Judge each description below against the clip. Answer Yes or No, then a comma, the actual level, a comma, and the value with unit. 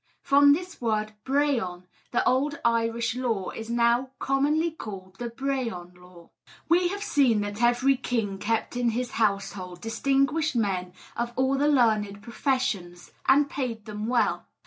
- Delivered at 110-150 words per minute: Yes, average, 145 wpm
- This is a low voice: No, high, 235 Hz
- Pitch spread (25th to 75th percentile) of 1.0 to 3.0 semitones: No, average, 4.7 semitones